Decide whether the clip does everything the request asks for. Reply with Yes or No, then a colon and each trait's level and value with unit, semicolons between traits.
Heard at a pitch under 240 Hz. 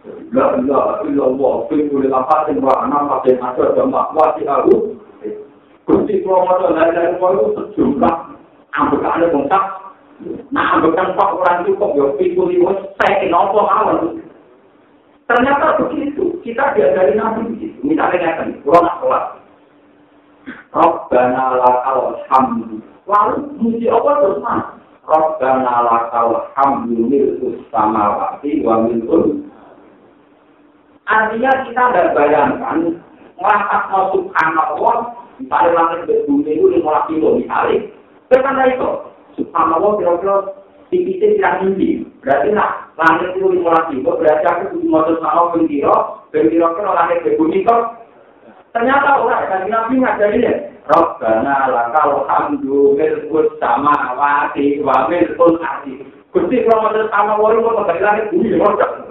Yes: high, 190 Hz